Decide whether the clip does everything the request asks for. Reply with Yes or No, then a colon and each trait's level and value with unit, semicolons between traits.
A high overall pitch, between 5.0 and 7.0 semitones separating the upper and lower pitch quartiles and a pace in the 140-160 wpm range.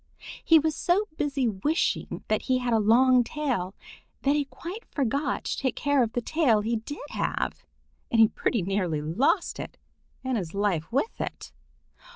No: very high, 255 Hz; average, 5.3 semitones; average, 175 wpm